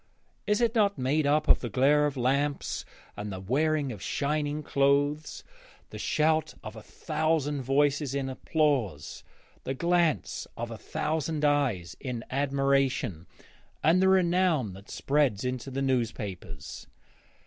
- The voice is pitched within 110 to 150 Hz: Yes, medium, 140 Hz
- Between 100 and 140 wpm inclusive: Yes, slow, 135 wpm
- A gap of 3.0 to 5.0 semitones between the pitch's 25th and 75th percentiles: Yes, average, 3.4 semitones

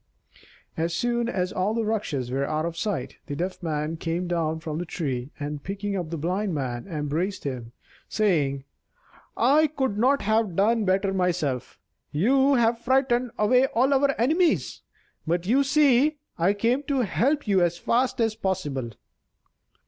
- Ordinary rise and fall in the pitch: No, wide, 6.9 semitones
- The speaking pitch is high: Yes, high, 195 Hz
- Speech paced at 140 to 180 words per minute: Yes, average, 160 wpm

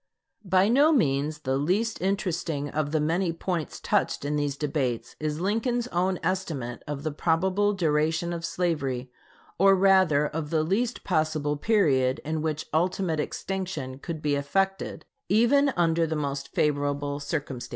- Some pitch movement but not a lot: Yes, average, 4.5 semitones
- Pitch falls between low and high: Yes, medium, 160 Hz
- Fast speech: No, average, 150 wpm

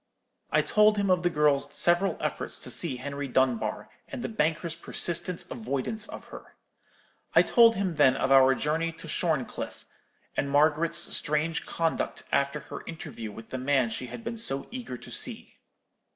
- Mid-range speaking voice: Yes, medium, 155 Hz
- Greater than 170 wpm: No, average, 165 wpm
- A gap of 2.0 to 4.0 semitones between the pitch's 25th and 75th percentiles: No, average, 4.9 semitones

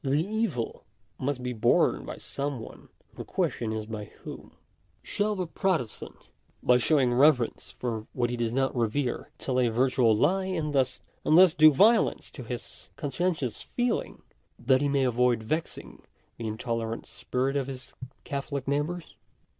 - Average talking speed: Yes, average, 155 wpm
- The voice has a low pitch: Yes, low, 130 Hz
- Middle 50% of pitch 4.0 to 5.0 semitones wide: Yes, average, 4.3 semitones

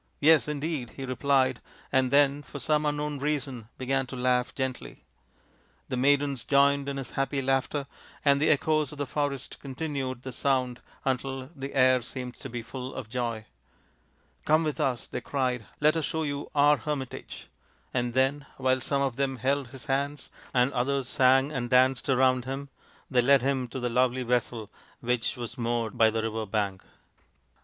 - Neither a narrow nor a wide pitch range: No, narrow, 2.1 semitones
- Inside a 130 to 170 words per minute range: No, average, 180 wpm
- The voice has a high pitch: No, low, 130 Hz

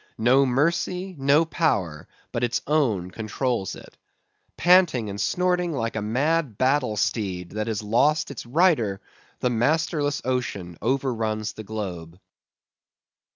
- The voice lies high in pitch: No, low, 125 Hz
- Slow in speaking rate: Yes, slow, 125 wpm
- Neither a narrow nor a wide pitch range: No, wide, 5.9 semitones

